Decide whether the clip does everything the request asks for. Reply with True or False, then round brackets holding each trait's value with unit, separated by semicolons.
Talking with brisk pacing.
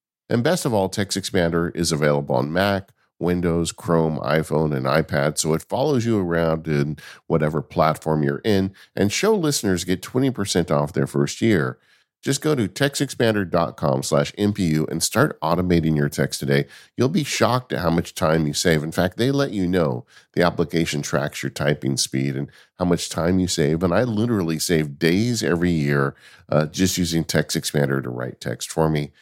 False (180 wpm)